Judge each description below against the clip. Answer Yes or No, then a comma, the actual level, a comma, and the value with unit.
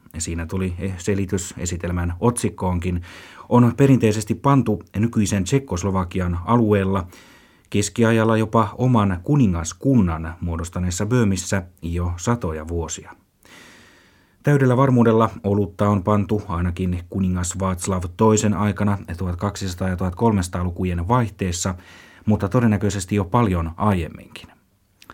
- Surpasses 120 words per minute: No, slow, 95 wpm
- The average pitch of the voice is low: Yes, low, 100 Hz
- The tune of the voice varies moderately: Yes, average, 3.6 semitones